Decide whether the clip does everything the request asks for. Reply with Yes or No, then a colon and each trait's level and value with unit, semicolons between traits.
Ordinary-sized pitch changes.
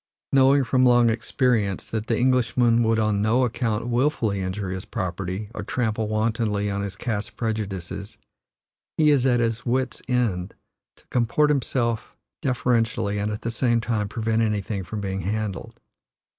Yes: average, 3.0 semitones